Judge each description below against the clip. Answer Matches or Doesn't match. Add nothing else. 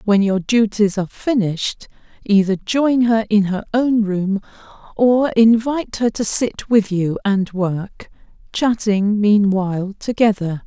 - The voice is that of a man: Doesn't match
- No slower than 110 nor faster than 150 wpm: Matches